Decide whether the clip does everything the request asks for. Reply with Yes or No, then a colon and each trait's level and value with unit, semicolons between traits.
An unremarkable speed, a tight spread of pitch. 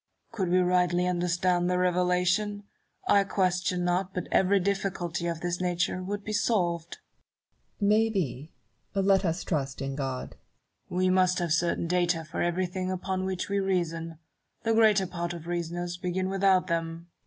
Yes: average, 160 wpm; narrow, 1.7 semitones